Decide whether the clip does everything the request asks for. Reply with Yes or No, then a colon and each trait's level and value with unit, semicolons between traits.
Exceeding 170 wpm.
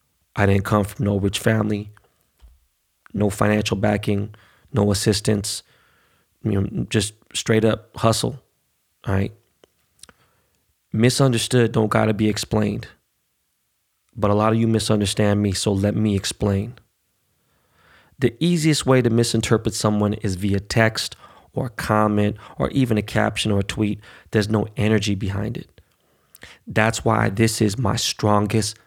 No: slow, 135 wpm